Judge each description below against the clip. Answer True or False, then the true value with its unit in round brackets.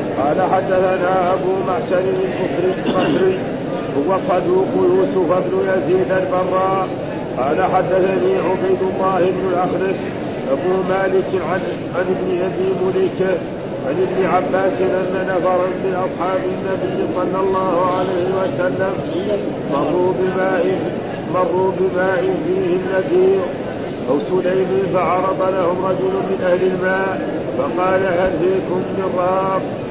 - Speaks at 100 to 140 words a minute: True (105 wpm)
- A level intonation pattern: True (0.6 semitones)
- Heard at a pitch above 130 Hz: True (185 Hz)